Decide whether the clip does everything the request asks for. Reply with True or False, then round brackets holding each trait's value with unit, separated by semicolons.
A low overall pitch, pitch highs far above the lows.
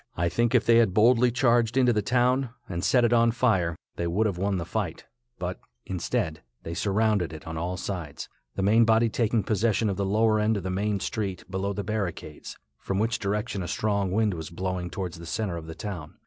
False (100 Hz; 4.0 semitones)